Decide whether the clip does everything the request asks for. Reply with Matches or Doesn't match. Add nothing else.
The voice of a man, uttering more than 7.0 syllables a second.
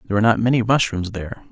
Matches